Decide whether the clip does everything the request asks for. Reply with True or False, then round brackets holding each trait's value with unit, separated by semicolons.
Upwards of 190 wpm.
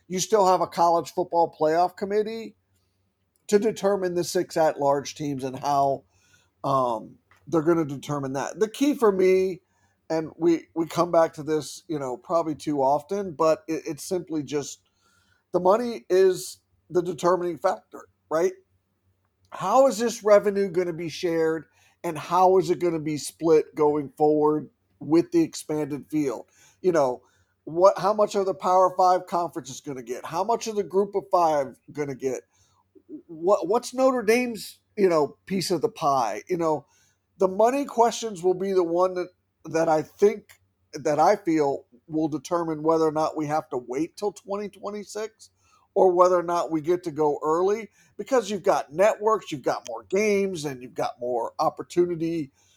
False (175 wpm)